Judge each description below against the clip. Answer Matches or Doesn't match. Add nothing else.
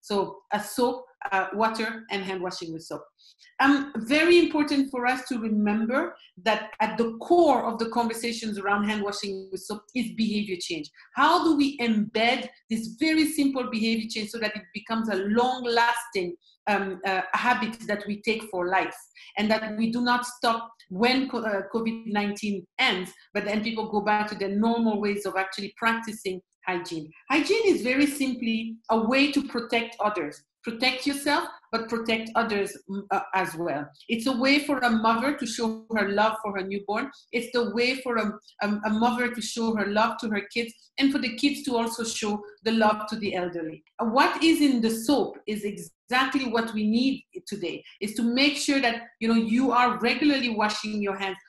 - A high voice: Matches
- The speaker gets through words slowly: Doesn't match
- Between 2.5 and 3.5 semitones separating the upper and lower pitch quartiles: Matches